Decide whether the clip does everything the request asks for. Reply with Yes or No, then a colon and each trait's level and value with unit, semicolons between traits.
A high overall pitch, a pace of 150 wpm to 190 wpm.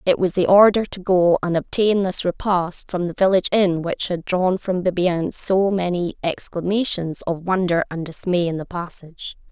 No: medium, 180 Hz; average, 185 wpm